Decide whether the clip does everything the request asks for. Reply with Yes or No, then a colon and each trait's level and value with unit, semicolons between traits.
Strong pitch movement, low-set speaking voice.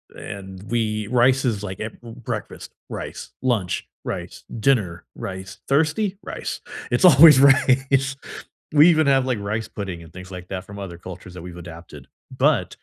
Yes: wide, 6.3 semitones; low, 110 Hz